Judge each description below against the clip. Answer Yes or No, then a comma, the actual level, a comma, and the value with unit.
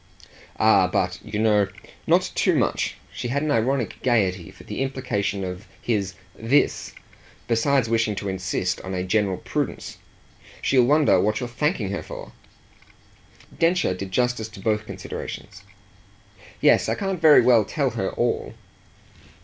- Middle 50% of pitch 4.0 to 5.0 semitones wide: Yes, average, 4.6 semitones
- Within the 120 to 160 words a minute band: Yes, average, 145 wpm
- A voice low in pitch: Yes, low, 110 Hz